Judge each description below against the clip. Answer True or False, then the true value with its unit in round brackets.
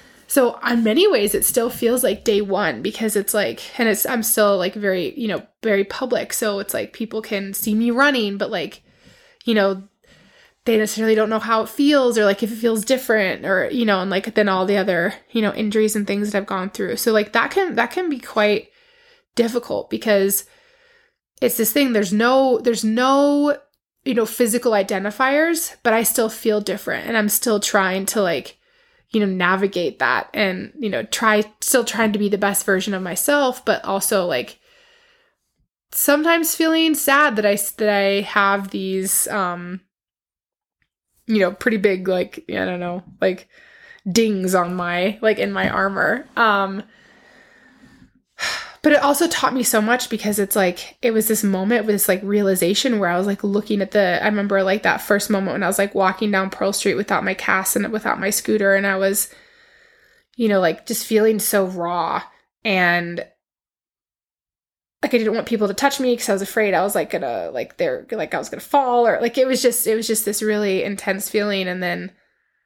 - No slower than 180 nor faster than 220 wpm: True (195 wpm)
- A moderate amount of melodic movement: True (4.2 semitones)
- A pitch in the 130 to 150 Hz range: False (215 Hz)